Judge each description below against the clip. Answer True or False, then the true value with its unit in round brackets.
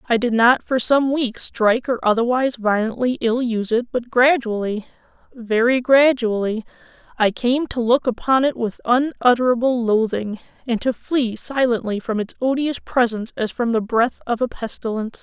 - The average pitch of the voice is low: False (240 Hz)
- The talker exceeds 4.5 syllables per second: True (4.9 syllables/s)